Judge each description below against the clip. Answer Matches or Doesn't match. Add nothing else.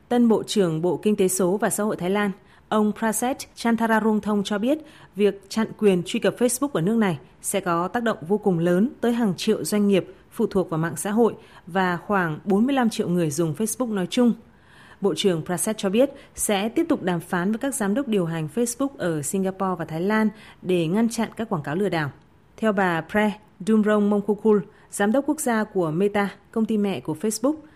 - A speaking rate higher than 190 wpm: Matches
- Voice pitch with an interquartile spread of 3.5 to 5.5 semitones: Doesn't match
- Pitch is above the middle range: Matches